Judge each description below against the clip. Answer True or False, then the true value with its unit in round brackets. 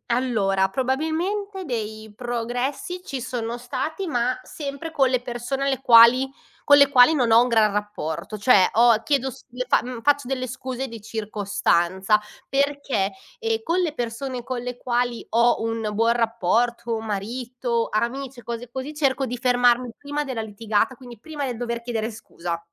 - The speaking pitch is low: False (245 Hz)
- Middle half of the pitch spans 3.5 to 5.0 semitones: False (2.9 semitones)